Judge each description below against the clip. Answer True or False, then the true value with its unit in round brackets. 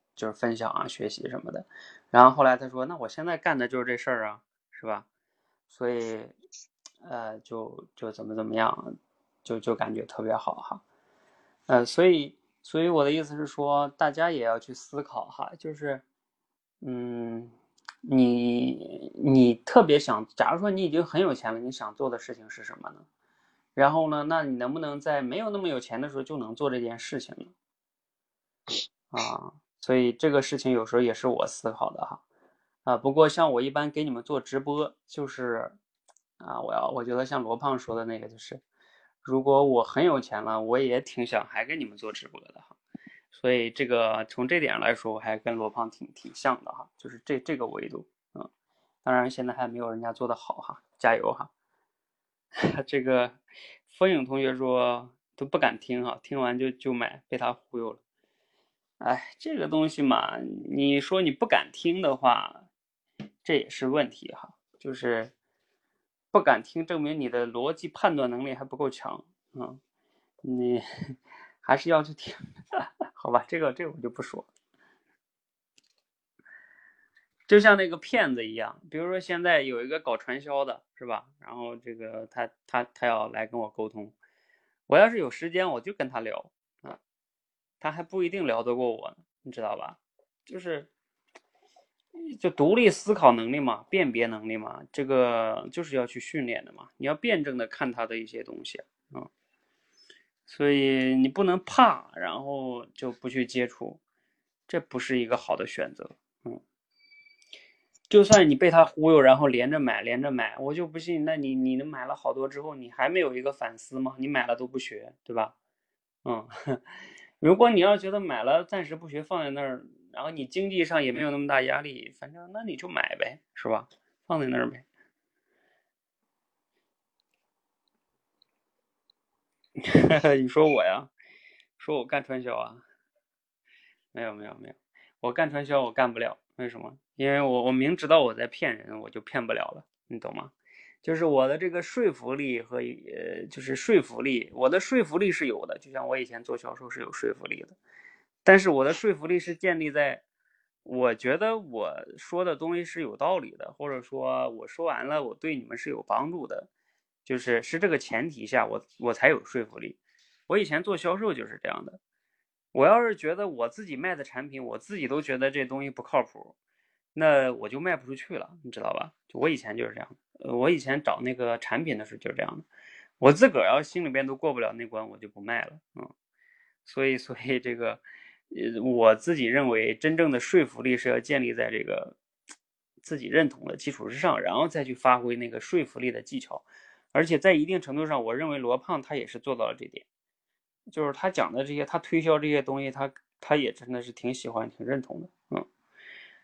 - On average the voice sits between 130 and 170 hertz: True (135 Hz)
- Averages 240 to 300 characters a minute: True (260 characters per minute)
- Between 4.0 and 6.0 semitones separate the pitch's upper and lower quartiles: True (5.2 semitones)